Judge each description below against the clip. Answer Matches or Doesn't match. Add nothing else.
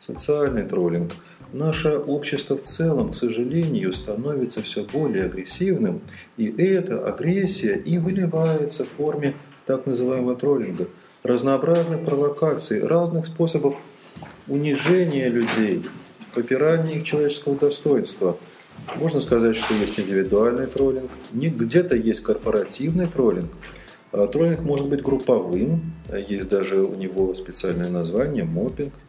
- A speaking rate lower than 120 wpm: Matches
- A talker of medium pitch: Matches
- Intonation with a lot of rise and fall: Doesn't match